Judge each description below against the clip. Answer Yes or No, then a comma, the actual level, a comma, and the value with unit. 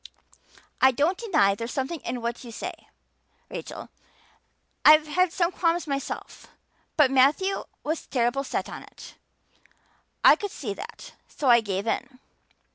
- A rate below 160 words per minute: Yes, average, 140 wpm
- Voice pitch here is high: Yes, very high, 275 Hz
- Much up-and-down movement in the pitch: Yes, wide, 5.9 semitones